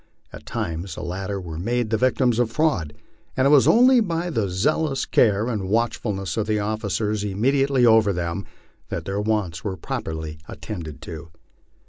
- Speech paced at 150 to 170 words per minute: Yes, average, 165 wpm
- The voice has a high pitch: No, low, 105 Hz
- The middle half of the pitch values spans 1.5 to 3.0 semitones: No, average, 4.8 semitones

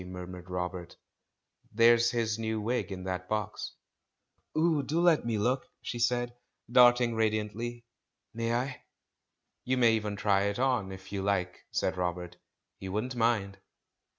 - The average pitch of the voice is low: Yes, low, 110 Hz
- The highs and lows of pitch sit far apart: No, average, 4.0 semitones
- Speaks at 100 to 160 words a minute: Yes, average, 150 wpm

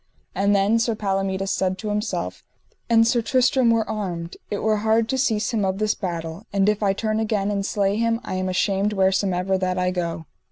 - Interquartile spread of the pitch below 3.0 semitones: Yes, narrow, 2.5 semitones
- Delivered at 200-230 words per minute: Yes, fast, 205 wpm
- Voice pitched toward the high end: Yes, high, 200 Hz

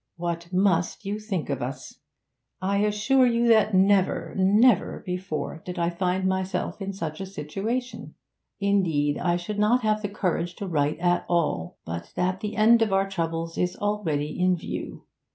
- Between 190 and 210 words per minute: No, average, 170 wpm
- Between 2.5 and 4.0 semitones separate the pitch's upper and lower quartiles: Yes, average, 3.5 semitones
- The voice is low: No, medium, 185 Hz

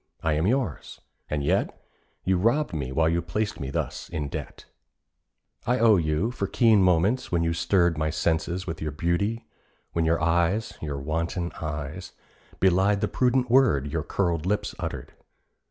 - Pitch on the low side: Yes, very low, 85 Hz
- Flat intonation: No, average, 4.8 semitones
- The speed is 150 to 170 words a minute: Yes, average, 165 wpm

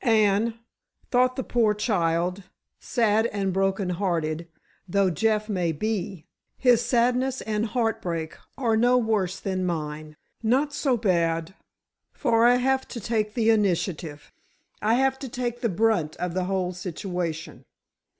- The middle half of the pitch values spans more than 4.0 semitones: Yes, average, 4.8 semitones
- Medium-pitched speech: No, high, 210 Hz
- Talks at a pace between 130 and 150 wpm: Yes, average, 140 wpm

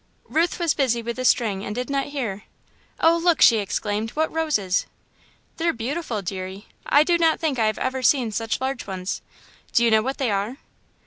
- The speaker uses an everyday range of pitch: No, wide, 5.9 semitones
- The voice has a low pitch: No, high, 245 Hz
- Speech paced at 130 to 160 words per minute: No, average, 195 wpm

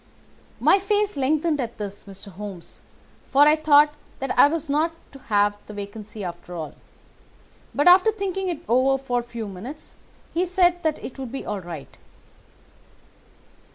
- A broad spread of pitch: Yes, wide, 7.8 semitones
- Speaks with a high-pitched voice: Yes, very high, 270 Hz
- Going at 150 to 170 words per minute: Yes, average, 160 wpm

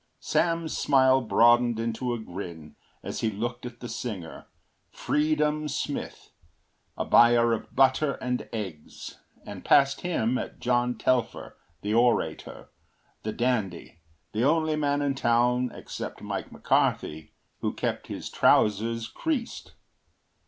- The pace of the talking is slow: Yes, slow, 125 wpm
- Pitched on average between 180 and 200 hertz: No, low, 120 Hz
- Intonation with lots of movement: No, average, 3.5 semitones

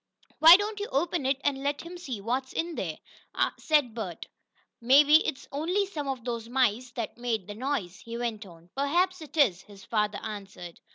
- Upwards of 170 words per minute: Yes, average, 185 wpm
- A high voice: Yes, very high, 255 Hz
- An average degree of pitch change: No, wide, 6.0 semitones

